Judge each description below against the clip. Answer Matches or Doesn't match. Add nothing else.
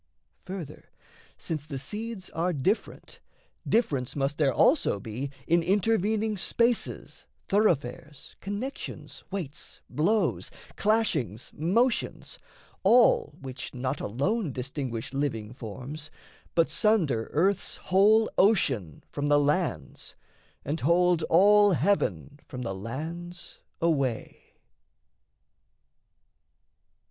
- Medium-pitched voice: Matches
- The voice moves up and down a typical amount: Doesn't match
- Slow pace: Matches